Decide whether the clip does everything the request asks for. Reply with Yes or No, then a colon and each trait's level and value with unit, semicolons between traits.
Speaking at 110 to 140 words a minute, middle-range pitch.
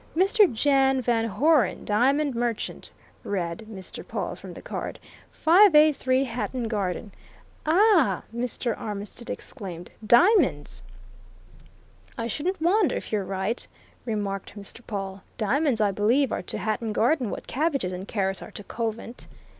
No: slow, 135 wpm; high, 235 Hz